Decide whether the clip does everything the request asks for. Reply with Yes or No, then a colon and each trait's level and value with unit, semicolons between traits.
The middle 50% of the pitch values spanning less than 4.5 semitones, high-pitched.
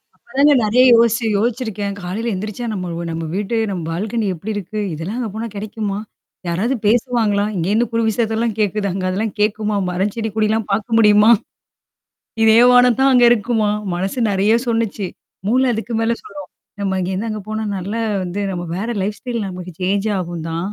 Yes: average, 3.0 semitones; high, 210 Hz